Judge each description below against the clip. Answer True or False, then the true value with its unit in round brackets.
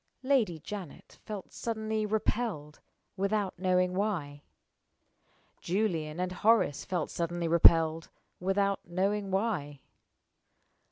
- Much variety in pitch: False (4.0 semitones)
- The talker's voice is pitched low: False (185 Hz)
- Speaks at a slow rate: True (95 wpm)